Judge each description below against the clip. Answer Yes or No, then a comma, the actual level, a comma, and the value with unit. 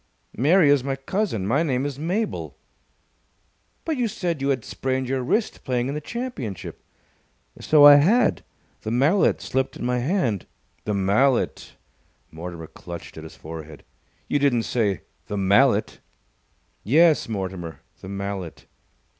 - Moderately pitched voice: No, low, 130 Hz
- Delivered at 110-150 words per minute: Yes, average, 140 wpm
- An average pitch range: No, wide, 6.9 semitones